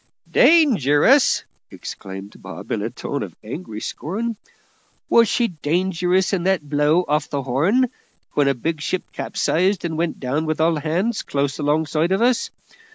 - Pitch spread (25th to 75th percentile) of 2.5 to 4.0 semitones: No, average, 4.6 semitones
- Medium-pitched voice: Yes, medium, 160 Hz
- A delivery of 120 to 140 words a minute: No, average, 155 wpm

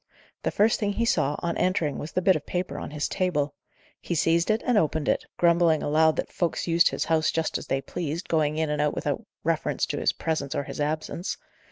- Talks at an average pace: No, fast, 220 wpm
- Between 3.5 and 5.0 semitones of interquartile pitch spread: No, average, 2.8 semitones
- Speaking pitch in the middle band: Yes, medium, 160 Hz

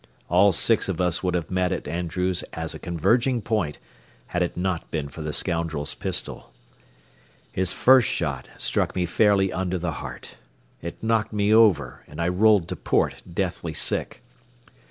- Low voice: Yes, very low, 90 Hz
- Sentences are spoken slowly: No, average, 165 wpm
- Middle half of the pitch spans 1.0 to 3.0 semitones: No, average, 3.5 semitones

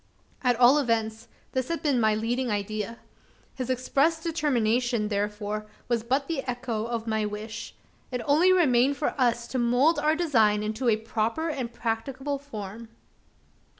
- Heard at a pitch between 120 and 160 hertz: No, high, 240 Hz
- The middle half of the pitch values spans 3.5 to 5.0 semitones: Yes, average, 3.9 semitones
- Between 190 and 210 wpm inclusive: No, average, 150 wpm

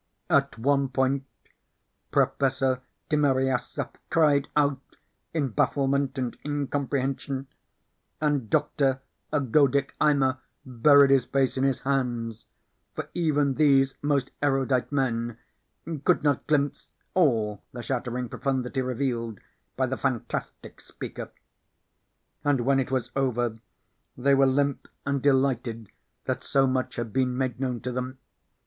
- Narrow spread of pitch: Yes, narrow, 1.8 semitones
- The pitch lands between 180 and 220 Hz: No, low, 135 Hz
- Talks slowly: Yes, slow, 120 wpm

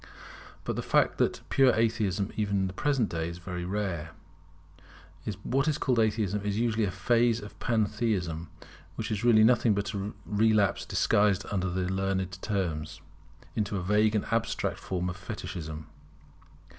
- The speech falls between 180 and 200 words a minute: No, average, 155 wpm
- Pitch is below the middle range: Yes, low, 100 Hz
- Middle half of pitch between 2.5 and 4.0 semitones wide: Yes, average, 3.3 semitones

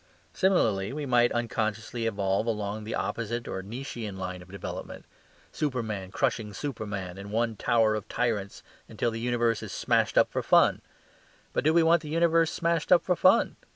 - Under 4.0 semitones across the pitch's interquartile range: No, average, 5.0 semitones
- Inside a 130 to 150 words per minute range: No, average, 170 wpm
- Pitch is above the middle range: No, low, 115 Hz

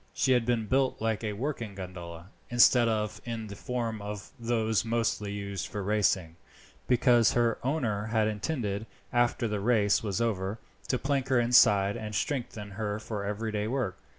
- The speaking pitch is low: Yes, low, 110 Hz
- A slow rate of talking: No, average, 165 wpm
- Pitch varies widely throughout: No, average, 2.8 semitones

